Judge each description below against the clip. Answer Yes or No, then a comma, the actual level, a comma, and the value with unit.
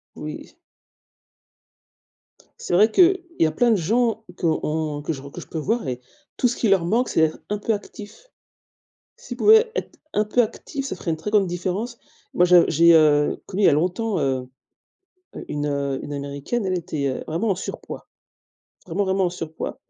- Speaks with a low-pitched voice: No, medium, 180 Hz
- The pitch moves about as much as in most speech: No, wide, 6.2 semitones